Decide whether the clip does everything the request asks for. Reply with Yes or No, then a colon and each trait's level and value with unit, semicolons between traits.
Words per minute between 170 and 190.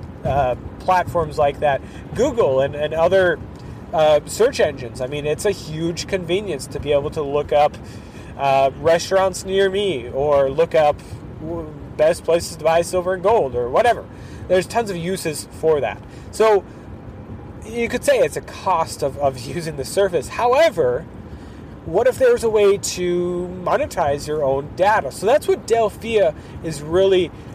No: average, 160 wpm